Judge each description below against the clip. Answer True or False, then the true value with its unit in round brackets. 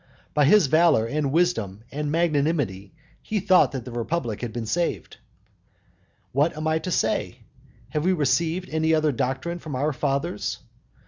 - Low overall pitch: False (150 Hz)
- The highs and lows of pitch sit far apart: False (4.4 semitones)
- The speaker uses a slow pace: False (155 wpm)